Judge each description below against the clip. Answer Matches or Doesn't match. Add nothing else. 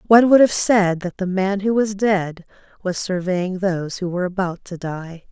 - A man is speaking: Doesn't match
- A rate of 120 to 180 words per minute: Doesn't match